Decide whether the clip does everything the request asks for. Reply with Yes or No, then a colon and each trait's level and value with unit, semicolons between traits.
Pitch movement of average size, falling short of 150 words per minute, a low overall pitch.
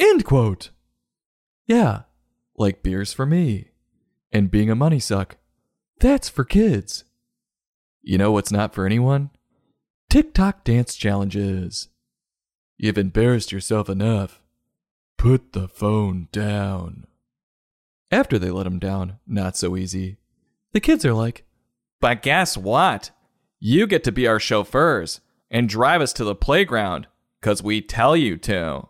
Yes: average, 4.2 semitones; slow, 135 wpm; low, 105 Hz